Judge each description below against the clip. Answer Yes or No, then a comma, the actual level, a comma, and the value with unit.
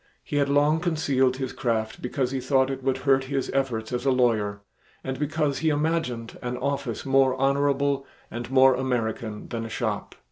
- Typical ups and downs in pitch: No, narrow, 2.3 semitones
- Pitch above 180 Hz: No, low, 130 Hz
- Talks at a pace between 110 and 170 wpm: No, average, 180 wpm